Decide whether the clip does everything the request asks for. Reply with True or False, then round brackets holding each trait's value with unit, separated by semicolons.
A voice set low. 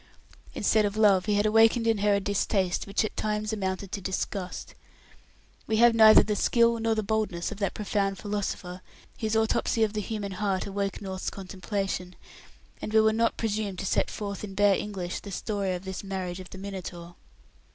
False (205 Hz)